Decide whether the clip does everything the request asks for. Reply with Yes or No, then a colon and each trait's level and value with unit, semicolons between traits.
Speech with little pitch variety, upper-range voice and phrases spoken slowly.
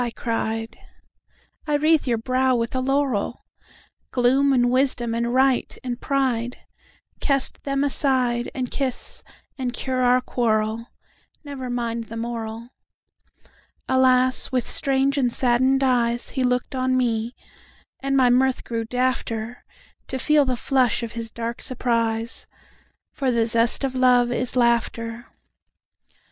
Yes: narrow, 2.0 semitones; very high, 250 Hz; slow, 115 wpm